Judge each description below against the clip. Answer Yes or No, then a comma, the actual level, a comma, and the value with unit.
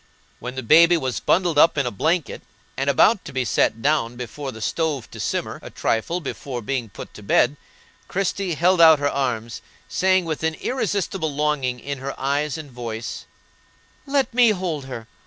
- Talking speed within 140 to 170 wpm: No, average, 180 wpm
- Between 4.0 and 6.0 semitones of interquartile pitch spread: Yes, average, 5.1 semitones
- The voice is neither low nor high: Yes, medium, 145 Hz